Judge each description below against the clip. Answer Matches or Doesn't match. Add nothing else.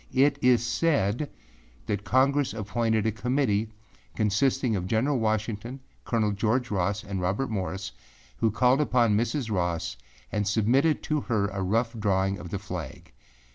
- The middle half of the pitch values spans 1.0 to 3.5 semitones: Doesn't match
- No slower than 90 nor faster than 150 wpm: Matches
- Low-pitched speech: Matches